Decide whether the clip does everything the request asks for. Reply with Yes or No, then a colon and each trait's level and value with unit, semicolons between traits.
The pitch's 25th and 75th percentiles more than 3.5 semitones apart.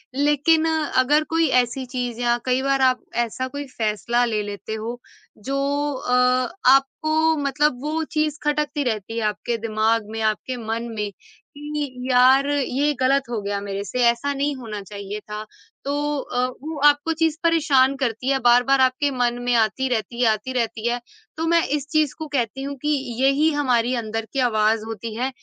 Yes: average, 4.1 semitones